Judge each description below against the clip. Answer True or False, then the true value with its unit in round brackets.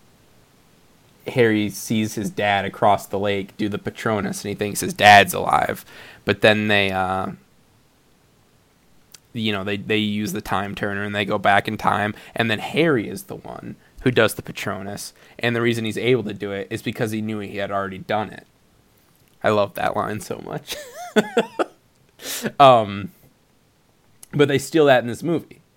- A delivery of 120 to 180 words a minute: True (175 wpm)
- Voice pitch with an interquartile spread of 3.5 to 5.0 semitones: False (2.9 semitones)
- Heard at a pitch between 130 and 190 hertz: False (105 Hz)